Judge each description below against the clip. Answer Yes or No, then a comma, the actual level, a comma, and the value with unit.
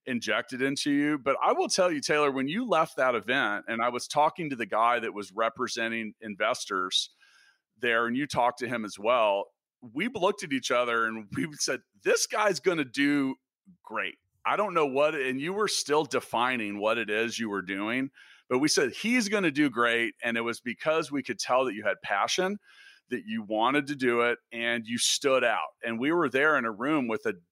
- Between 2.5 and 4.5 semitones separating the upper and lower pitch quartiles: No, average, 5.0 semitones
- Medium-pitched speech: No, low, 130 Hz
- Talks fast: Yes, fast, 220 wpm